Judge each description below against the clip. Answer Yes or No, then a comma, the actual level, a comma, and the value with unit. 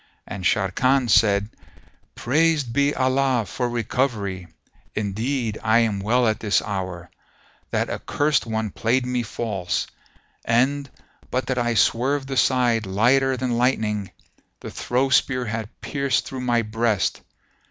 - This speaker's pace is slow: Yes, slow, 130 wpm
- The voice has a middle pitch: No, low, 120 Hz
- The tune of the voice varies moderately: Yes, average, 3.4 semitones